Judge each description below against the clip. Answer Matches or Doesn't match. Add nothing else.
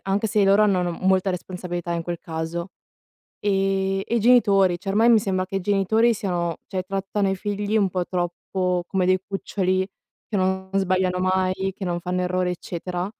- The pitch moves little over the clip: Matches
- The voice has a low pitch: Doesn't match